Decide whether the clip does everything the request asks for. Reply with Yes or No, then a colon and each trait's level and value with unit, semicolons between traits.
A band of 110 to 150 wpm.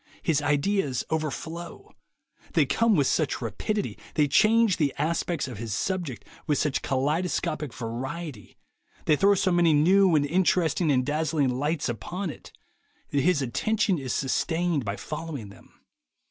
Yes: average, 145 wpm